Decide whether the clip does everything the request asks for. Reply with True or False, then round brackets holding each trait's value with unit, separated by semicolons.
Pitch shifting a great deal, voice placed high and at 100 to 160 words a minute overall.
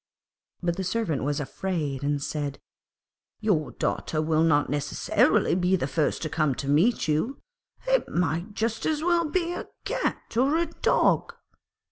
False (7.6 semitones; 170 Hz; 155 wpm)